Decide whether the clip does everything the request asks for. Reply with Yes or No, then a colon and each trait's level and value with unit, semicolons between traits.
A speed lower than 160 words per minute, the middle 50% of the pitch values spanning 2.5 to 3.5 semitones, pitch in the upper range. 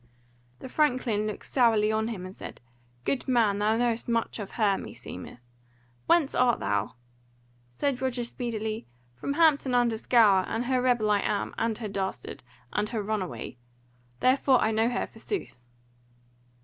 Yes: average, 150 wpm; average, 3.1 semitones; high, 225 Hz